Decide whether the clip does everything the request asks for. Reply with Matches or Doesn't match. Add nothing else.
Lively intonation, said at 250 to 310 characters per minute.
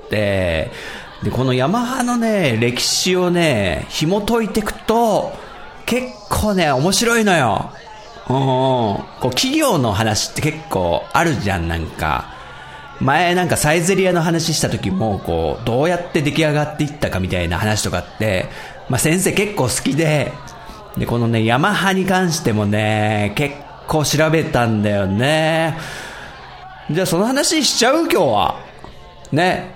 Matches